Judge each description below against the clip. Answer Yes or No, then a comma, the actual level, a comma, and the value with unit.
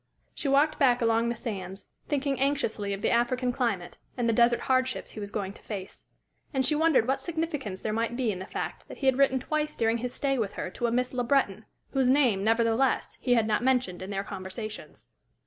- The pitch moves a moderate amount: Yes, average, 4.0 semitones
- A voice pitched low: No, high, 240 Hz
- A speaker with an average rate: No, fast, 225 wpm